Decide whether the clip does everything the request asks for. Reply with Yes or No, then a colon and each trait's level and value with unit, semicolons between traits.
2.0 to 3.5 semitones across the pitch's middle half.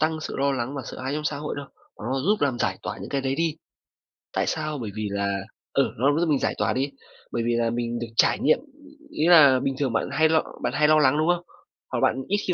No: average, 4.3 semitones